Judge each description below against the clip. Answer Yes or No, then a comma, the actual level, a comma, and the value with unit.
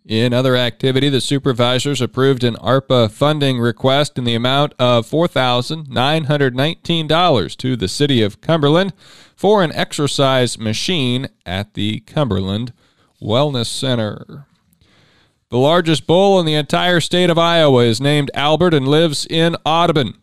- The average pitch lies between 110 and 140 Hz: Yes, low, 135 Hz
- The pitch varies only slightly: No, average, 4.4 semitones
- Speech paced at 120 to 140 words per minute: Yes, slow, 135 wpm